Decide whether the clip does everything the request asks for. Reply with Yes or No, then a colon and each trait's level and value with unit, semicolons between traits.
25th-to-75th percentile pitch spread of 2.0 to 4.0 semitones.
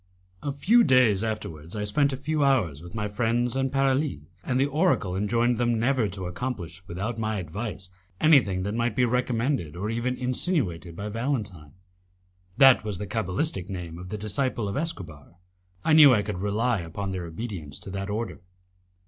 No: wide, 5.5 semitones